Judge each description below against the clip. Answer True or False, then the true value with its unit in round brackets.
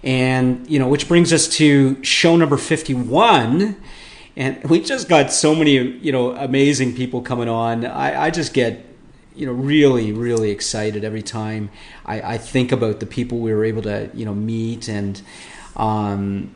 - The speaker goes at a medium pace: True (175 wpm)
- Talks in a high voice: False (125 Hz)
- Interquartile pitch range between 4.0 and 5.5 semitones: True (4.6 semitones)